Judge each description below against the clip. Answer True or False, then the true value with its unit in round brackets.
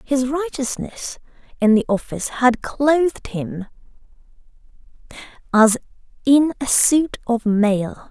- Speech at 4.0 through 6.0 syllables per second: False (3.7 syllables/s)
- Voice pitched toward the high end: True (245 Hz)